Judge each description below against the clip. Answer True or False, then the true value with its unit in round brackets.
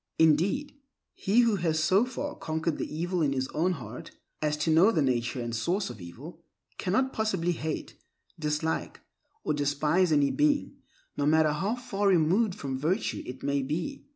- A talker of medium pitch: True (160 Hz)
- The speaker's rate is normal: True (170 wpm)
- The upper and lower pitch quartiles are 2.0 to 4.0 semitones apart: False (4.8 semitones)